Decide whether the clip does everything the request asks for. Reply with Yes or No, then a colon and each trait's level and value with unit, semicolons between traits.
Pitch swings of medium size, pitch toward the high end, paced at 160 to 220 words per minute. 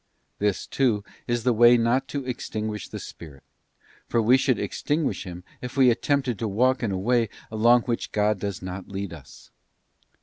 No: average, 3.8 semitones; low, 115 Hz; average, 180 wpm